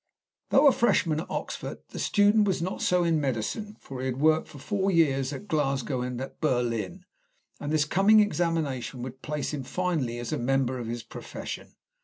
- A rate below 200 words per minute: Yes, average, 190 wpm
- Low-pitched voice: No, medium, 150 Hz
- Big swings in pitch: Yes, wide, 5.8 semitones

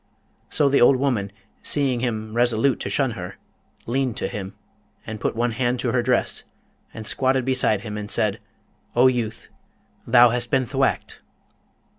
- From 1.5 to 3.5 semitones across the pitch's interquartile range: Yes, average, 2.8 semitones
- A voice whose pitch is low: Yes, low, 120 Hz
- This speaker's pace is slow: No, average, 160 wpm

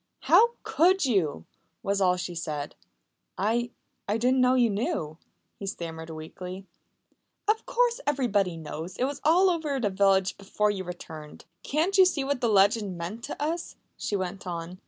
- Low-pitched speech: No, high, 200 Hz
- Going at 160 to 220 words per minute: Yes, average, 165 wpm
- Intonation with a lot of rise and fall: Yes, wide, 7.6 semitones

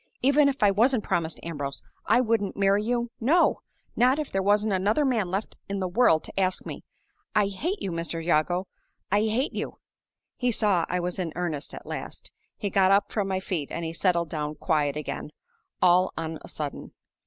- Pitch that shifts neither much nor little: Yes, average, 4.6 semitones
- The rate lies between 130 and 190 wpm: No, average, 200 wpm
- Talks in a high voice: Yes, high, 195 Hz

